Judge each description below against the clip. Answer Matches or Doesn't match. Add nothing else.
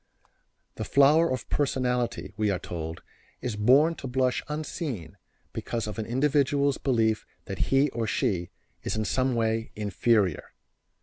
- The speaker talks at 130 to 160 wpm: Matches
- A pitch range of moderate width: Matches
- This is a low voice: Matches